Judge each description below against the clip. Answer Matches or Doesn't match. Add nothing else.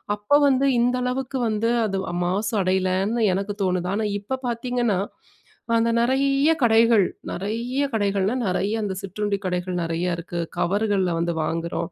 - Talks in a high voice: Matches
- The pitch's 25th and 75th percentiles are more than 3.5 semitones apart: Matches